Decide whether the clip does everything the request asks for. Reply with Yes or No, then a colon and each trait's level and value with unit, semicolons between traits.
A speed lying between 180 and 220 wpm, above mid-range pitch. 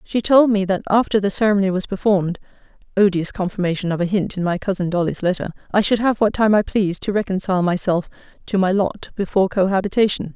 Yes: average, 195 wpm; high, 195 Hz